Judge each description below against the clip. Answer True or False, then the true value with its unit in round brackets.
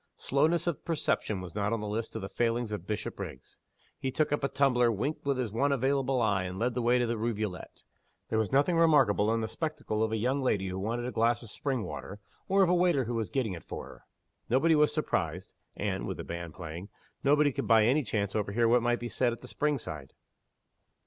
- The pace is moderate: False (230 wpm)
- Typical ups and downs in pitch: True (4.9 semitones)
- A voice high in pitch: False (120 Hz)